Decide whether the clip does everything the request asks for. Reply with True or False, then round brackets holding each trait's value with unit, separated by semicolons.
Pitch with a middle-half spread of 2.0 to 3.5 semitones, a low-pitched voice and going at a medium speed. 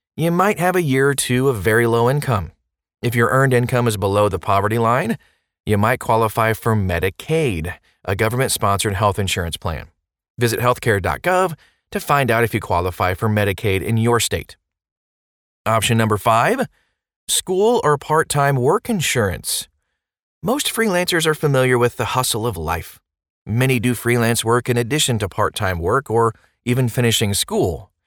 False (4.6 semitones; 115 Hz; 160 wpm)